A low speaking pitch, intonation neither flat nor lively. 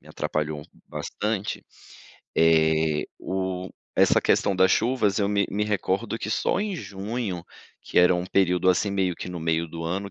Yes: very low, 95 Hz; average, 3.4 semitones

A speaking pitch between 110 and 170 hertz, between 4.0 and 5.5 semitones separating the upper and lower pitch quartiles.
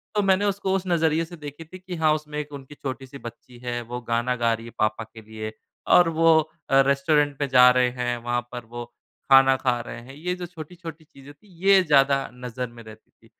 Yes: low, 135 Hz; average, 4.8 semitones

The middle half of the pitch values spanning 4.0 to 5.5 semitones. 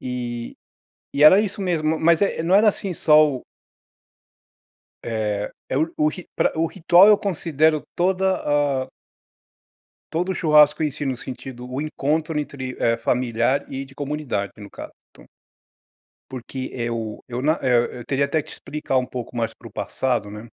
Yes: average, 4.6 semitones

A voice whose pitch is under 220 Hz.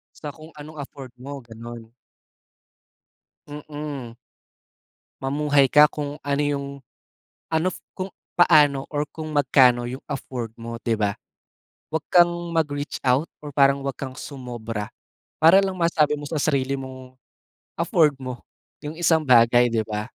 Yes: medium, 140 Hz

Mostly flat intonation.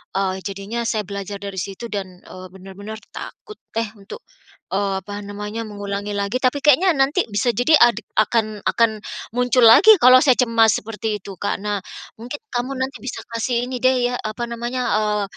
No: average, 3.5 semitones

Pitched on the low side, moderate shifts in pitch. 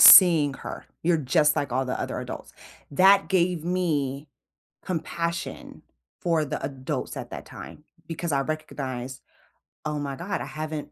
No: medium, 155 Hz; average, 3.7 semitones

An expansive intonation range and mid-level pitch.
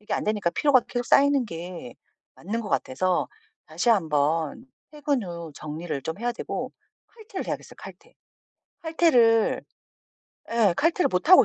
No: wide, 8.5 semitones; high, 210 Hz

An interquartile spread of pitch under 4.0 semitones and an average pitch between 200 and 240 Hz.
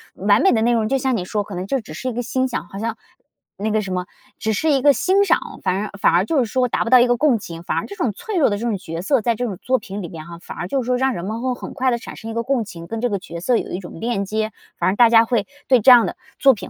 No: average, 4.5 semitones; high, 225 Hz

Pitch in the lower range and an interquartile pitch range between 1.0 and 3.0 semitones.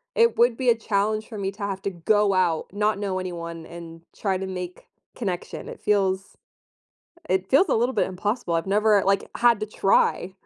No: high, 195 Hz; narrow, 2.6 semitones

